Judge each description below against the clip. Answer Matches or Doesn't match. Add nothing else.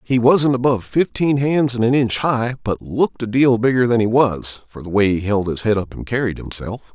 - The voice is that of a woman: Doesn't match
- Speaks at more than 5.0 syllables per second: Matches